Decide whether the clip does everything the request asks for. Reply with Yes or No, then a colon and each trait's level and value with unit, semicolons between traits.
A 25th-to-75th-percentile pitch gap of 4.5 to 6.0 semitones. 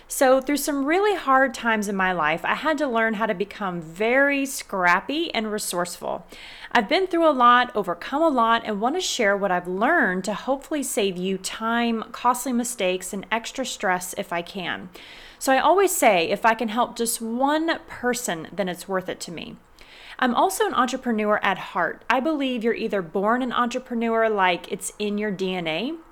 Yes: average, 5.1 semitones